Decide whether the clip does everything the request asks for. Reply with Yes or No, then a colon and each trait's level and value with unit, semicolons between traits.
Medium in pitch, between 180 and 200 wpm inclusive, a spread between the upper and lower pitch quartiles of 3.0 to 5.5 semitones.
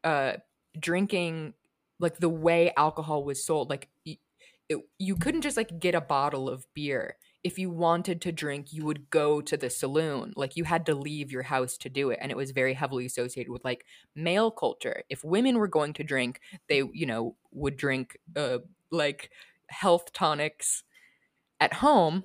Yes: medium, 155 Hz; average, 185 wpm; average, 4.1 semitones